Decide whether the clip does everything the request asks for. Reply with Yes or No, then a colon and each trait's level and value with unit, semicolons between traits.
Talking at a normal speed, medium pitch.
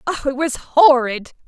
No: average, 165 wpm; very high, 275 Hz